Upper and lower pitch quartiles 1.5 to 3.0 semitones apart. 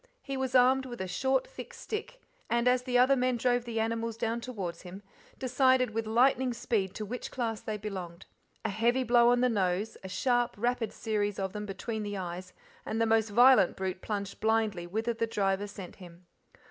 No: average, 3.7 semitones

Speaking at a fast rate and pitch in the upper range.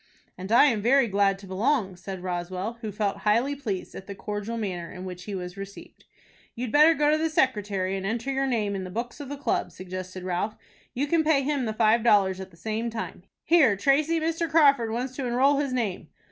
Yes: fast, 220 wpm; high, 220 Hz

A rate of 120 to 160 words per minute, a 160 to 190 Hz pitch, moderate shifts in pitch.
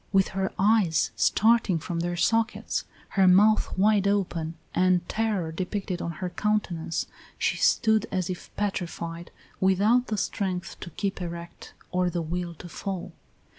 Yes: average, 145 wpm; medium, 185 Hz; average, 3.1 semitones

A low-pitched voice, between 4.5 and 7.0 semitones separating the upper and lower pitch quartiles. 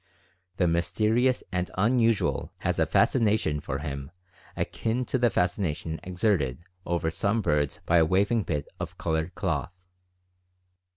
Yes: very low, 90 Hz; wide, 5.6 semitones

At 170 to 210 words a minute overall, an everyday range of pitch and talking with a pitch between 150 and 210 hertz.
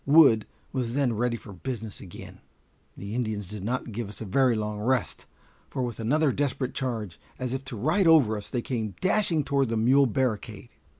No: average, 190 wpm; average, 3.8 semitones; low, 120 Hz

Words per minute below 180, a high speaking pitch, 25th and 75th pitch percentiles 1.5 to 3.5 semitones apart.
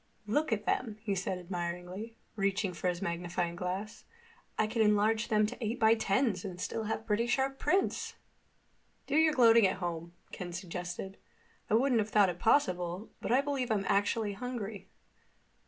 No: average, 170 wpm; high, 210 Hz; average, 4.0 semitones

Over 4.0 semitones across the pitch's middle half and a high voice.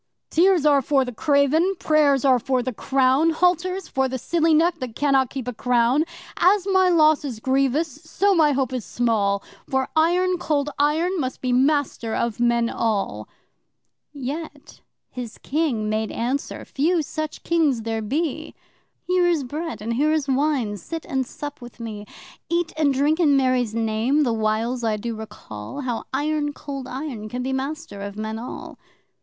Yes: average, 4.7 semitones; very high, 270 Hz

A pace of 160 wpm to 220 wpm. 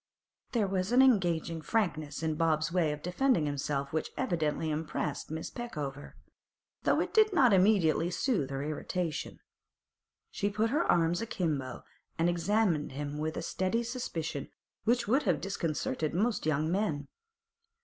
No: average, 150 wpm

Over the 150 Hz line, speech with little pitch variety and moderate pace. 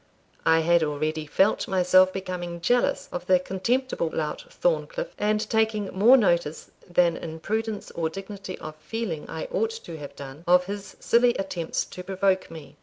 No: medium, 185 Hz; average, 4.7 semitones; average, 165 wpm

